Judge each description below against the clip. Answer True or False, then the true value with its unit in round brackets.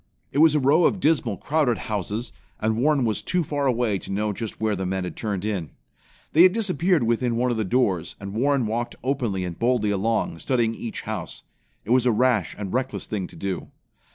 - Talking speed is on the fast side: True (210 wpm)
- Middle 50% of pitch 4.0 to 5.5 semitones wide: True (4.4 semitones)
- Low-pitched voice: True (115 Hz)